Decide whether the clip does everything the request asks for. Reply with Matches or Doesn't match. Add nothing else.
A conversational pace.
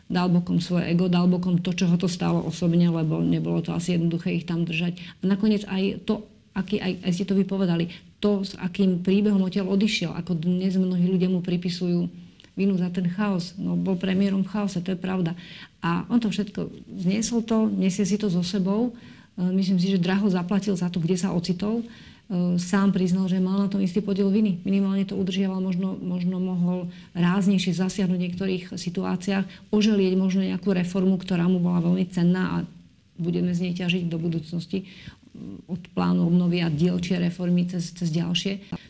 Doesn't match